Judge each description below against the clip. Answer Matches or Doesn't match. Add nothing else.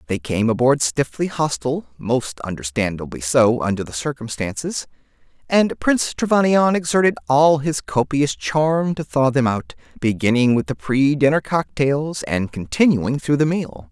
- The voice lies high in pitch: Doesn't match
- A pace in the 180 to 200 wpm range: Doesn't match